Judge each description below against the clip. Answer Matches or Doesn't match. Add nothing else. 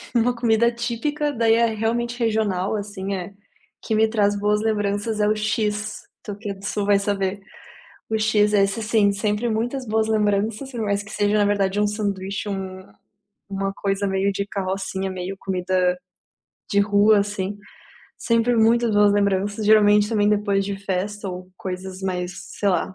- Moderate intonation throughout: Doesn't match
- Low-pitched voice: Doesn't match